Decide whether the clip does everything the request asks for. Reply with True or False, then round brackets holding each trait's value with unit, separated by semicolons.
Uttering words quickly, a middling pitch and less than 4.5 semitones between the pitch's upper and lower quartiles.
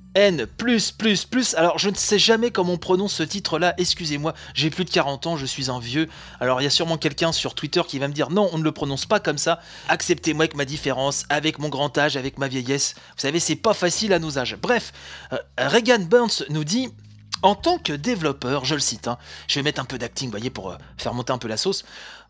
False (245 wpm; 155 Hz; 5.1 semitones)